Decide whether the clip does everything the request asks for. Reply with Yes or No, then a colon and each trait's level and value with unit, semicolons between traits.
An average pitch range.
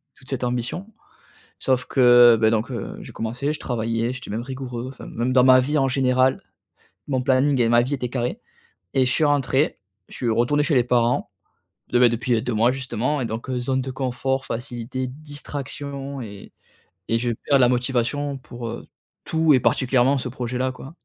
No: narrow, 1.9 semitones